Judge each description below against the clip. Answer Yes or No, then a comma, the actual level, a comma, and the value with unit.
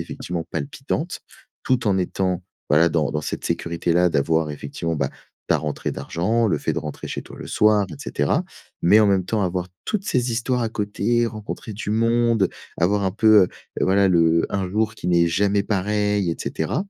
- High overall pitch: No, low, 100 Hz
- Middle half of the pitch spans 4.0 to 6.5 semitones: Yes, average, 4.4 semitones